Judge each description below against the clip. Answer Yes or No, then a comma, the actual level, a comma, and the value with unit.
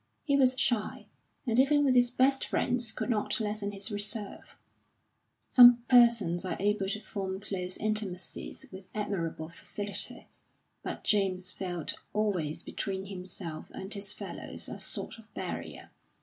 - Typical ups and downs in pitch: Yes, average, 3.8 semitones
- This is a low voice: No, high, 205 Hz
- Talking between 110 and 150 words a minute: Yes, average, 140 wpm